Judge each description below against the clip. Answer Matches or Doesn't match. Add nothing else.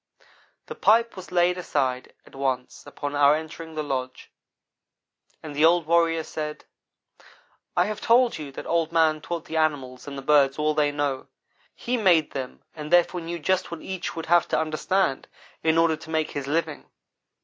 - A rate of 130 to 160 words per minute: Doesn't match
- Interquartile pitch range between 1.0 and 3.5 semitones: Matches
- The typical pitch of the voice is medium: Matches